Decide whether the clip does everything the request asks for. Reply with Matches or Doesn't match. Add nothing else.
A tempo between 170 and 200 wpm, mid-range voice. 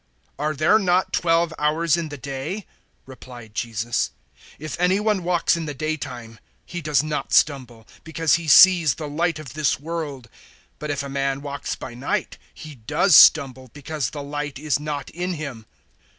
Matches